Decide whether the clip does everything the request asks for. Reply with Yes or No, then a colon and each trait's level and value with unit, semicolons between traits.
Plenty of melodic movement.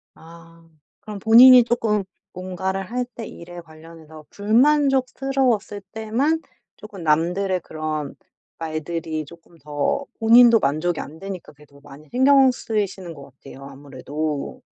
Yes: wide, 6.4 semitones